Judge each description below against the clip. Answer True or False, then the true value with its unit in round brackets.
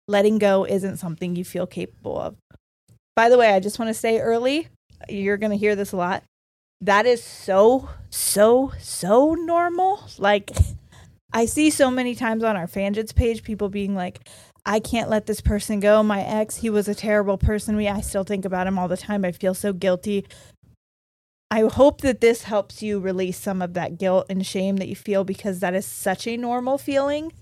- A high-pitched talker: True (205 Hz)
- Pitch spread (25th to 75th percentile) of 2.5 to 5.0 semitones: True (3.1 semitones)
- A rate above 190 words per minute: True (200 wpm)